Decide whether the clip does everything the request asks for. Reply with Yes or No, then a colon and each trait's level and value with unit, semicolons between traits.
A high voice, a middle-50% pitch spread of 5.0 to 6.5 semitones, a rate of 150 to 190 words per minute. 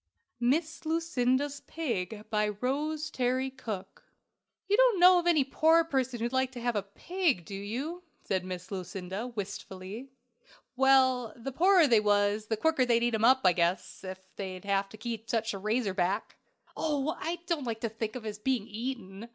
Yes: high, 235 Hz; average, 5.3 semitones; average, 175 wpm